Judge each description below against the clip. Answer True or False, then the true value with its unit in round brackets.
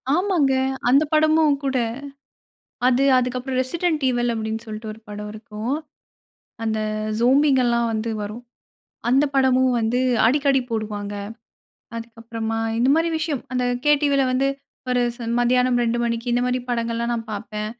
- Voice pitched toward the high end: True (245 Hz)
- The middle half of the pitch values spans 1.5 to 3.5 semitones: True (3.1 semitones)